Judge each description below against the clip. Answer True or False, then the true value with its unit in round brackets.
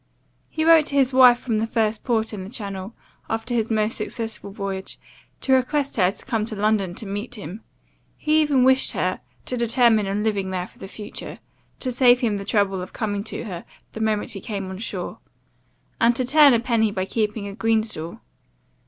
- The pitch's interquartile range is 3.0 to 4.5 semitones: True (3.5 semitones)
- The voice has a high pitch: True (220 Hz)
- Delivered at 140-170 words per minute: False (205 wpm)